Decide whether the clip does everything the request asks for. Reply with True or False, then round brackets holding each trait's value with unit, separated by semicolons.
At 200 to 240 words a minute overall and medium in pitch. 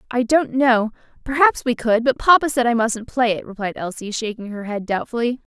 False (205 wpm; 235 Hz)